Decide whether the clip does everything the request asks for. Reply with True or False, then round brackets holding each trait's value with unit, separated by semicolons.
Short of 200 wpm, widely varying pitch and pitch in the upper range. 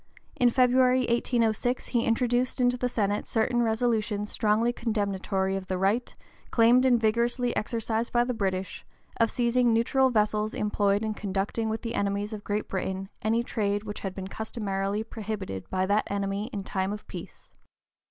False (170 wpm; 2.9 semitones; 220 Hz)